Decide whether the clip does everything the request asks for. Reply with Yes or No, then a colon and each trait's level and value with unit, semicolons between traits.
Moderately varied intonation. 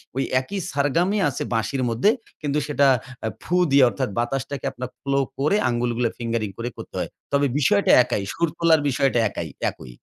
Yes: average, 3.5 semitones